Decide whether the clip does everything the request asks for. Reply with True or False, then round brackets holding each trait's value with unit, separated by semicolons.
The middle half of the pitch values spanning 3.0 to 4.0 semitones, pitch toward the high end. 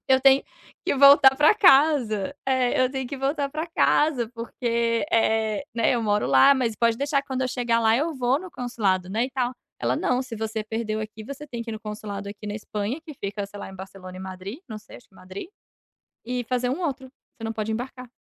True (3.7 semitones; 235 Hz)